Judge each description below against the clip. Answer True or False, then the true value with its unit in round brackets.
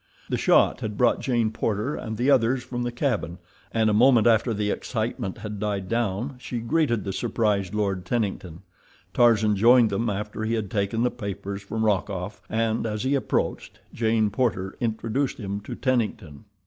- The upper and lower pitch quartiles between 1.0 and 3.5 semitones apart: True (2.8 semitones)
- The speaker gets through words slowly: False (175 wpm)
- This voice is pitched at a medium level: False (110 Hz)